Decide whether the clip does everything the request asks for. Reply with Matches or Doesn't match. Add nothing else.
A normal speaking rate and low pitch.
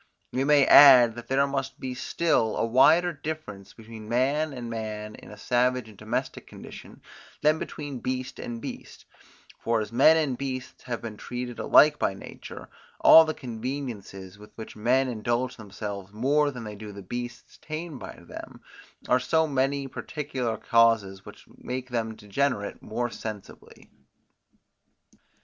Matches